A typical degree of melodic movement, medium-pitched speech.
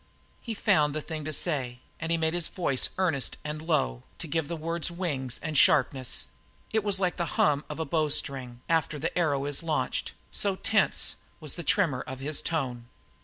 Yes: average, 3.5 semitones; medium, 155 Hz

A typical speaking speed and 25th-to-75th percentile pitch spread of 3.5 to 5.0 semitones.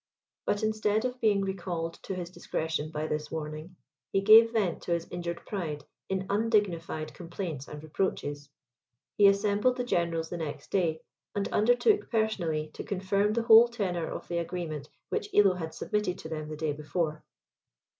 Yes: average, 165 wpm; average, 4.6 semitones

